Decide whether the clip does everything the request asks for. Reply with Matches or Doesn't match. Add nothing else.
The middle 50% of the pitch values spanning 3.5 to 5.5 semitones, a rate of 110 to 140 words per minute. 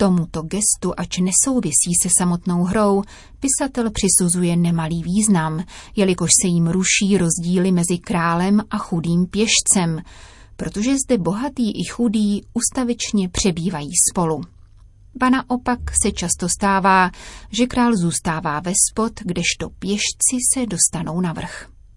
Matches